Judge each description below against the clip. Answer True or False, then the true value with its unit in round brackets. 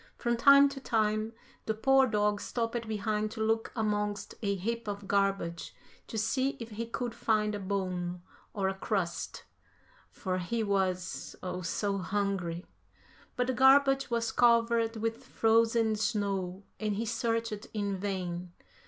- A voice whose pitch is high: True (215 Hz)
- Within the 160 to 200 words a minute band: False (145 wpm)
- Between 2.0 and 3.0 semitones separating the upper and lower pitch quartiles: True (2.7 semitones)